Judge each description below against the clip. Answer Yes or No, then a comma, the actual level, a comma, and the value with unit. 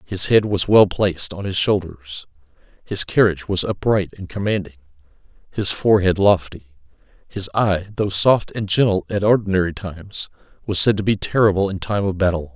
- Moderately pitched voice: No, very low, 95 Hz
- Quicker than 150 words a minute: Yes, average, 165 wpm